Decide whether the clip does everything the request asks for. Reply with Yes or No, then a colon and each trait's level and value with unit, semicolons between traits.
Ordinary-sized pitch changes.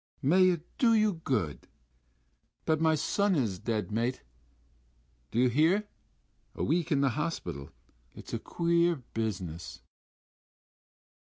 No: wide, 7.1 semitones